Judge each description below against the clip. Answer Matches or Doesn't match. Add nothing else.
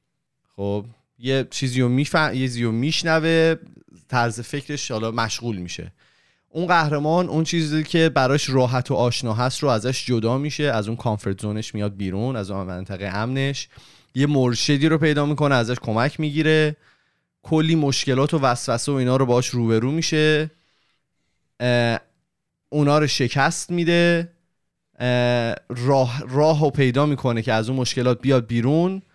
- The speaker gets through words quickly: Doesn't match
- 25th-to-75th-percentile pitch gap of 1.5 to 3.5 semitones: Doesn't match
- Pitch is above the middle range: Doesn't match